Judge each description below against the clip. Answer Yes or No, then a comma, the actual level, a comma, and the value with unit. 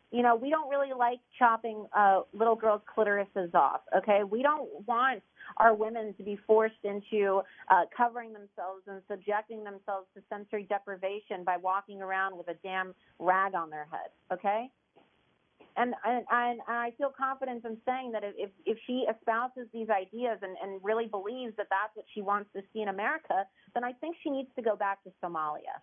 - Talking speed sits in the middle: Yes, average, 185 wpm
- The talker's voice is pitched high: Yes, high, 215 Hz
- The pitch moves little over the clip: No, average, 3.3 semitones